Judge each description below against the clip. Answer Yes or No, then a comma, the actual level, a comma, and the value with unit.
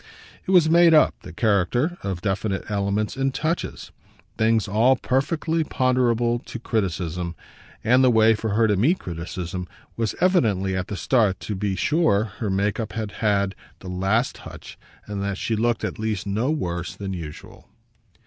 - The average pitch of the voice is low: Yes, low, 110 Hz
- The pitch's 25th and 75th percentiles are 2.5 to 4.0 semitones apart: No, average, 4.5 semitones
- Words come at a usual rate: Yes, average, 170 wpm